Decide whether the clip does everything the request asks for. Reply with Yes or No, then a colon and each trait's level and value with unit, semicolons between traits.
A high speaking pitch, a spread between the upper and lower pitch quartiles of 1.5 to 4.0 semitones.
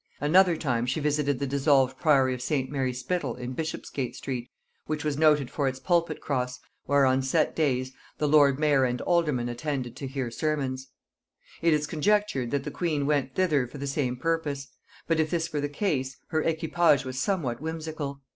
No: medium, 140 Hz; average, 3.2 semitones